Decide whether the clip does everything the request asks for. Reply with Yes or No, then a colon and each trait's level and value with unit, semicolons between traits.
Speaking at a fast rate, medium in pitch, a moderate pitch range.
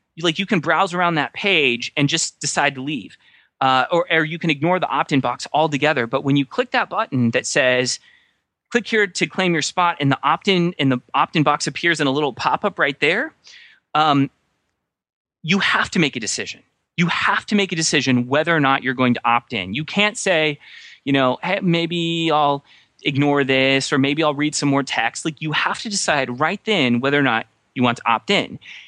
Yes: fast, 220 wpm; medium, 150 Hz; average, 4.3 semitones